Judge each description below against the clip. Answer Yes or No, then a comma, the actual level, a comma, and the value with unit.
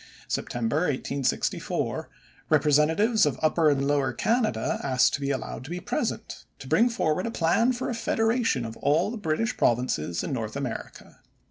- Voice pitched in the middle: Yes, medium, 150 Hz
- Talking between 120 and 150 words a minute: No, average, 160 wpm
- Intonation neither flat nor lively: No, wide, 8.6 semitones